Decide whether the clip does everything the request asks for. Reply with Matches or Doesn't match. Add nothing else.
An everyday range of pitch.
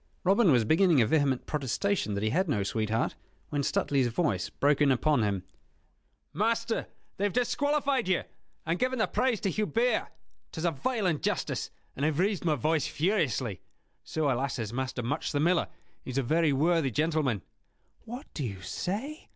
Doesn't match